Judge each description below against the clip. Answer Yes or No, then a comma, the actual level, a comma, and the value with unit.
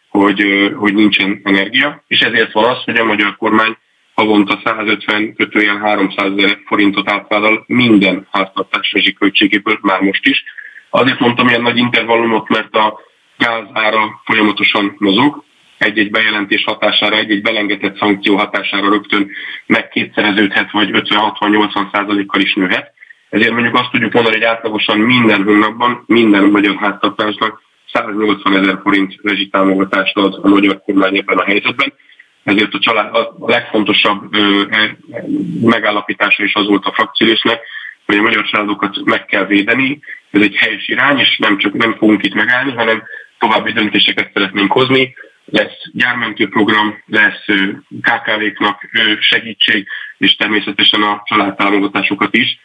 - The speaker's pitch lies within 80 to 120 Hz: Yes, low, 105 Hz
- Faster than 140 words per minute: No, average, 130 wpm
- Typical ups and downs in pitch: No, narrow, 1.8 semitones